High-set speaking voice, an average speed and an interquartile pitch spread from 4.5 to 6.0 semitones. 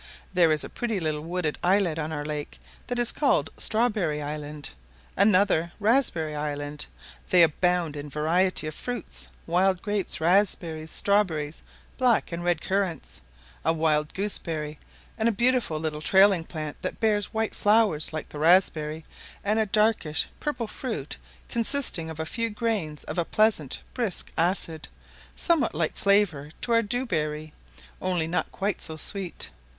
No: medium, 175 Hz; average, 155 wpm; average, 5.2 semitones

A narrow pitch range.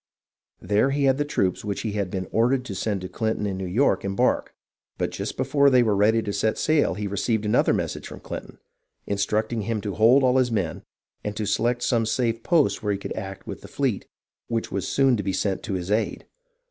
No: average, 3.5 semitones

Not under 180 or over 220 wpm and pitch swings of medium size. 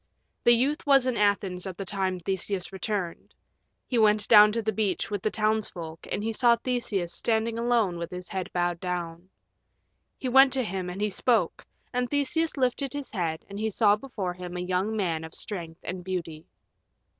Yes: average, 190 wpm; average, 4.4 semitones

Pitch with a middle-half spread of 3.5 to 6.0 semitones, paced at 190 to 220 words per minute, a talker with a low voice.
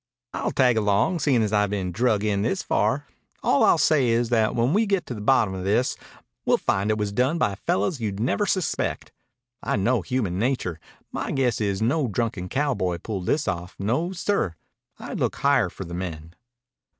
Yes: average, 5.0 semitones; average, 195 wpm; low, 110 Hz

